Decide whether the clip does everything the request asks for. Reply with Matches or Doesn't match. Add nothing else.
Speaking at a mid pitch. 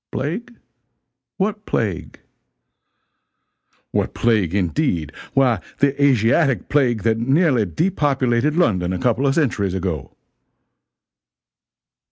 Doesn't match